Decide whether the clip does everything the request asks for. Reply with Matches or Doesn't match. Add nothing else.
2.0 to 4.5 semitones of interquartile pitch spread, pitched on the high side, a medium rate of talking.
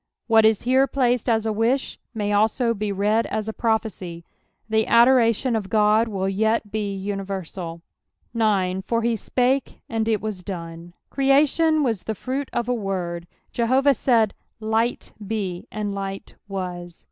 Matches